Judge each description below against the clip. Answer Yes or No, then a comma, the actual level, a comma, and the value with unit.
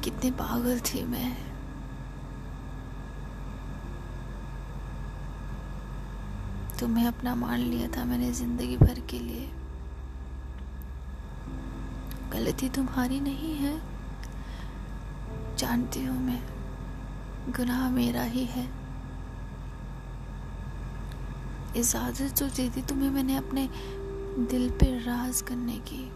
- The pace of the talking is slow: Yes, slow, 85 wpm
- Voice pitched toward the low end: Yes, low, 125 Hz